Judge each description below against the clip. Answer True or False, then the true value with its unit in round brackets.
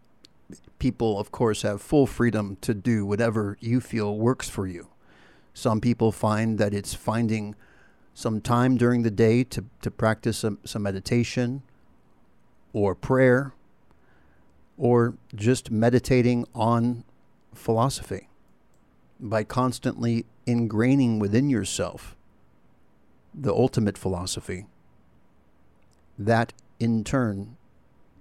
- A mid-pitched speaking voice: False (115 Hz)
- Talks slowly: True (105 wpm)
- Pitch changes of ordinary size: True (3.1 semitones)